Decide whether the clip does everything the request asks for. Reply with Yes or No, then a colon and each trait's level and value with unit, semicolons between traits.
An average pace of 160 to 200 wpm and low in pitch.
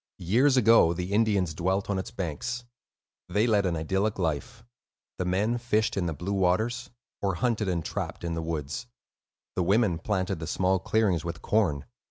Yes: average, 175 wpm; very low, 95 Hz